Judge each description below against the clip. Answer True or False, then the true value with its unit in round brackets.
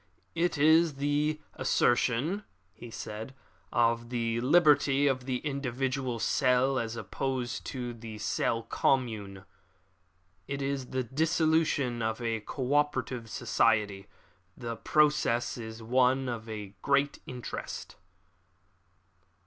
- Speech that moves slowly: True (110 wpm)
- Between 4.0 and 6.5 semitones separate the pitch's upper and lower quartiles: False (3.4 semitones)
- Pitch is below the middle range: True (125 Hz)